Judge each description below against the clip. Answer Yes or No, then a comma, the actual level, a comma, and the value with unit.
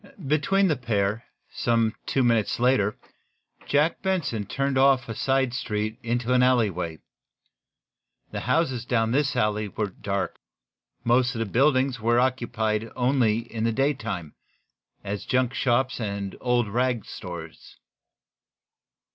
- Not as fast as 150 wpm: Yes, average, 140 wpm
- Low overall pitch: Yes, low, 120 Hz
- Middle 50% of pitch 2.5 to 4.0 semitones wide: Yes, average, 3.4 semitones